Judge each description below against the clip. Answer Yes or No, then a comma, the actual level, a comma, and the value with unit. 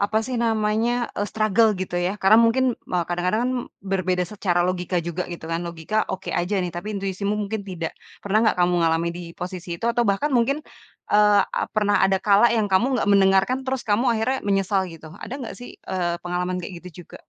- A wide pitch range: No, average, 3.3 semitones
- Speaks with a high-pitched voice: Yes, high, 195 Hz